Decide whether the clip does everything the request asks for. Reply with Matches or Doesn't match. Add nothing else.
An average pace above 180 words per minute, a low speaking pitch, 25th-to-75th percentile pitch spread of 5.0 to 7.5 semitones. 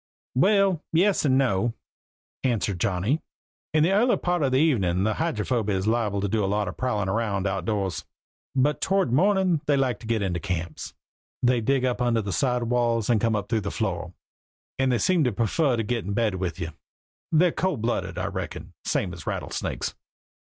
Matches